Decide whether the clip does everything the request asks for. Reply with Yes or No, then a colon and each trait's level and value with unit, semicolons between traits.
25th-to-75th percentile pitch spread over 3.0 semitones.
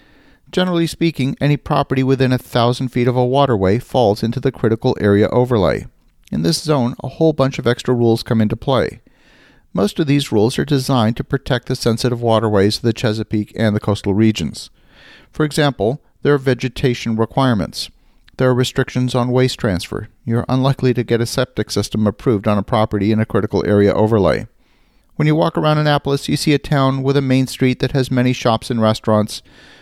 Yes: average, 3.5 semitones